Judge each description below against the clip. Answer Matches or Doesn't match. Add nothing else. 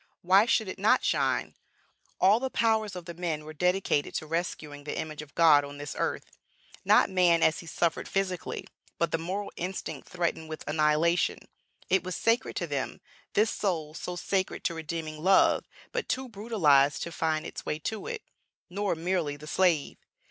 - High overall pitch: Doesn't match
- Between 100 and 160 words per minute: Doesn't match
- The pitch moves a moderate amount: Matches